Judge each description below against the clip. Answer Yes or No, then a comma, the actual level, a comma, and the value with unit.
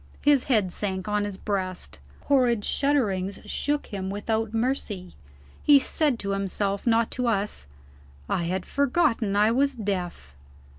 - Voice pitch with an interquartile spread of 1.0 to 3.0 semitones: No, average, 4.7 semitones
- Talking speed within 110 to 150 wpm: Yes, average, 140 wpm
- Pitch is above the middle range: Yes, high, 210 Hz